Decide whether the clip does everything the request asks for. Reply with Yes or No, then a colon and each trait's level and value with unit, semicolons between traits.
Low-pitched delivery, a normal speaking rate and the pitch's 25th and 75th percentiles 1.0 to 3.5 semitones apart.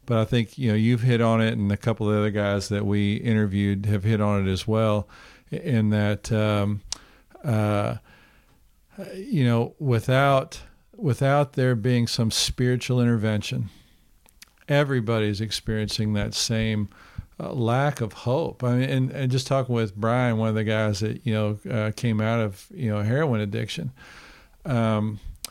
Yes: low, 110 Hz; average, 165 wpm; average, 3.0 semitones